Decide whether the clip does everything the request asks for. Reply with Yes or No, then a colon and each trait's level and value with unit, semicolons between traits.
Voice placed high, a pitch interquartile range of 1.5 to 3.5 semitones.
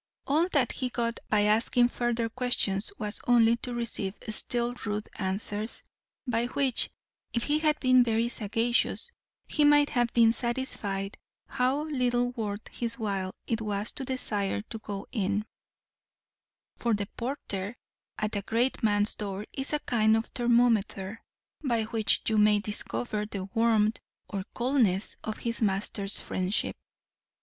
Yes: high, 225 Hz; average, 2.8 semitones